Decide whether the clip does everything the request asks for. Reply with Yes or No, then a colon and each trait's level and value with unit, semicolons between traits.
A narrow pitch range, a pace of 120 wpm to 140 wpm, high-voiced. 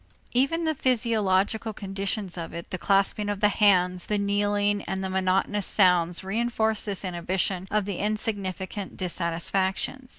Yes: narrow, 2.3 semitones; slow, 135 wpm; high, 200 Hz